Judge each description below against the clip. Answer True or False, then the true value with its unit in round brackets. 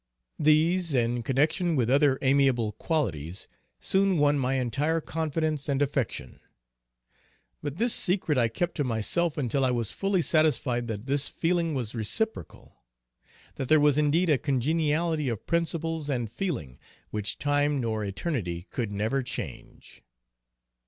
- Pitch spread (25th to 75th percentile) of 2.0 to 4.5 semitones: False (5.1 semitones)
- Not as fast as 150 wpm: True (140 wpm)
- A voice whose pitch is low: False (145 Hz)